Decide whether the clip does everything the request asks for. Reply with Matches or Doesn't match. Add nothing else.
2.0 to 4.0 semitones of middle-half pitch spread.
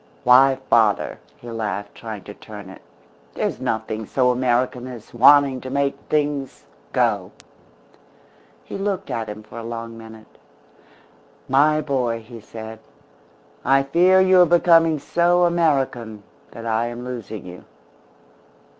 Doesn't match